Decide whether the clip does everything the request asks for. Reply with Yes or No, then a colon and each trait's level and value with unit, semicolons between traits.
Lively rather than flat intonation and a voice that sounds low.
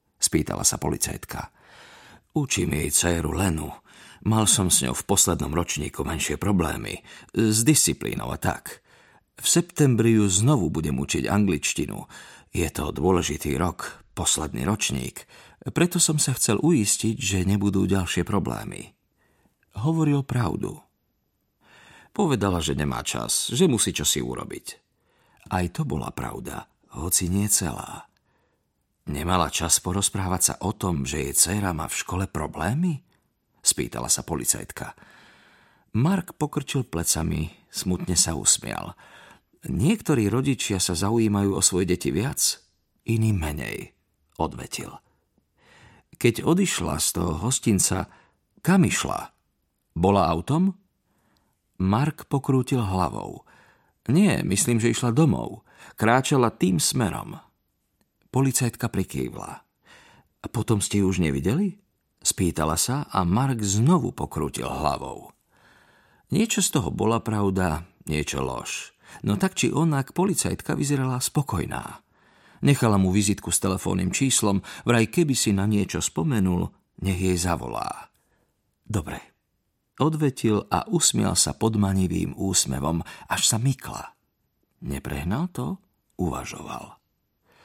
Yes: wide, 7.2 semitones; low, 100 Hz